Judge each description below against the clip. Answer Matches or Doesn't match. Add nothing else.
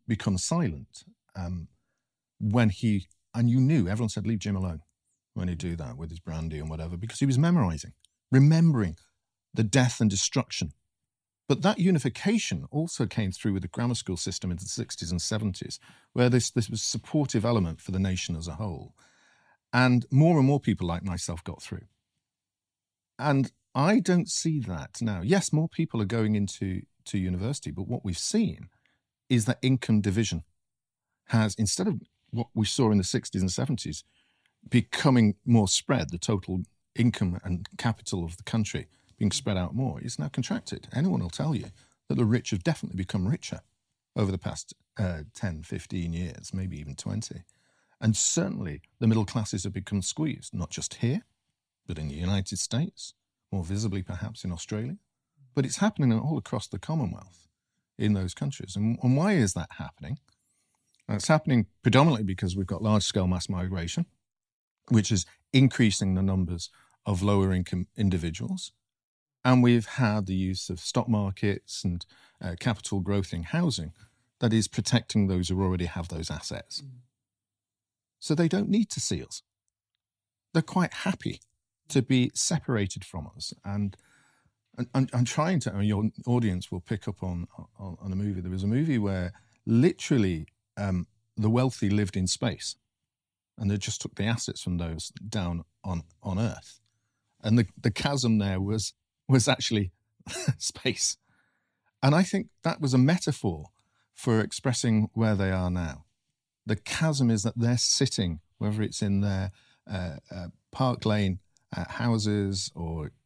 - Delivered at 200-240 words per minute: Doesn't match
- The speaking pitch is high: Doesn't match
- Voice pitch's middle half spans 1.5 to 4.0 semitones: Doesn't match